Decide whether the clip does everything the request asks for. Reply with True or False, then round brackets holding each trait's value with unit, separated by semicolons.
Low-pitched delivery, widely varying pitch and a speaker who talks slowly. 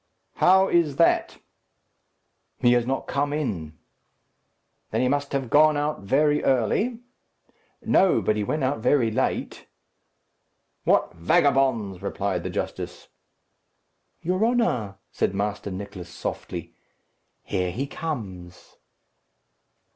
True (130 Hz; 7.0 semitones; 110 wpm)